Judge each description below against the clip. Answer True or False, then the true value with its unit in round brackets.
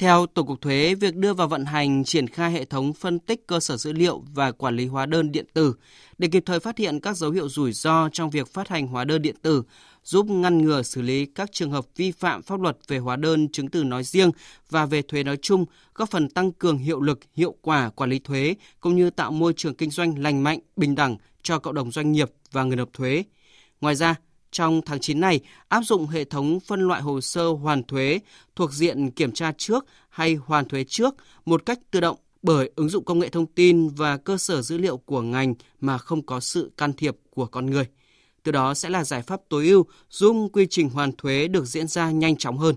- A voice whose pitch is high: False (155 Hz)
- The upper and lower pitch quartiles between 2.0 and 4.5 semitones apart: True (3.7 semitones)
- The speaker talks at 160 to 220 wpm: False (240 wpm)